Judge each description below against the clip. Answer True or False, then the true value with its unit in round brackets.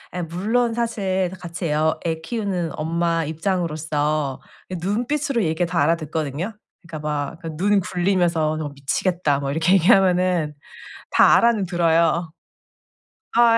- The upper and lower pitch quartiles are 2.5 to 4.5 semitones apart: True (3.4 semitones)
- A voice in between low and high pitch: True (170 Hz)